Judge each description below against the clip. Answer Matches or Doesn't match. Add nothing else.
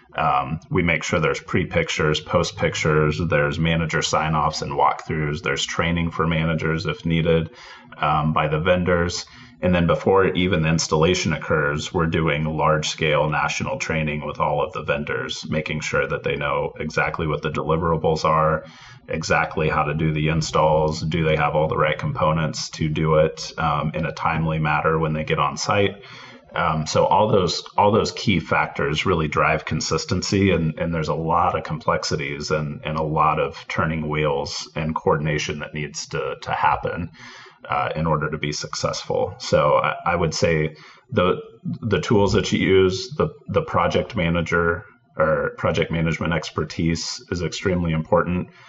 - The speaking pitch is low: Matches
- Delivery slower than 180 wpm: Matches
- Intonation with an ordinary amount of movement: Doesn't match